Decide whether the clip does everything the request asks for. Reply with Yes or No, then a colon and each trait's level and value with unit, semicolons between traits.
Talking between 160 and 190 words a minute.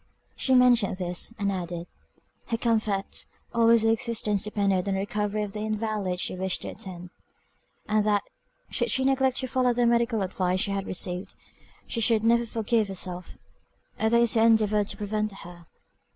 Yes: average, 170 wpm